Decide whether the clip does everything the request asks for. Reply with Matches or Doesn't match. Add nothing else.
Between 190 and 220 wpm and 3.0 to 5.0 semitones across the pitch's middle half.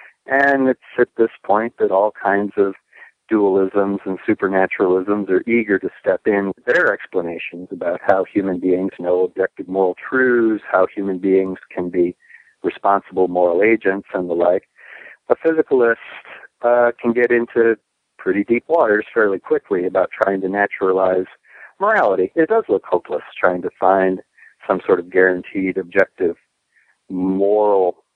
Doesn't match